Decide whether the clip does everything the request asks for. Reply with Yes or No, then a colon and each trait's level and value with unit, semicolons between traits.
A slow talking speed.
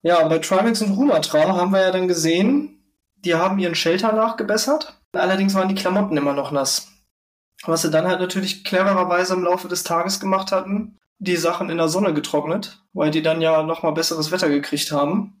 No: fast, 190 wpm